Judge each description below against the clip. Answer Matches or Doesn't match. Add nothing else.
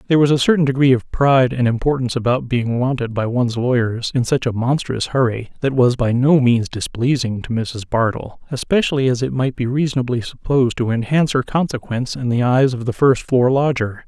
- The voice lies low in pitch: Matches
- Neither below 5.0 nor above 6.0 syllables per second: Matches